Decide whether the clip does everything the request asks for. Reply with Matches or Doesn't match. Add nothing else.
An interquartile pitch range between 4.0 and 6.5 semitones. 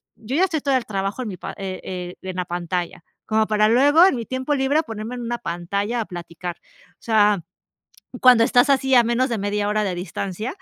Matches